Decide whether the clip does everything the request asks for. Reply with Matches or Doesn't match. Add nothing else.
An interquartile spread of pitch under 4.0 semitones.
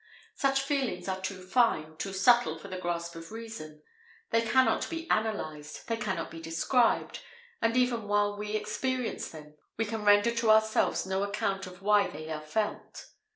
Doesn't match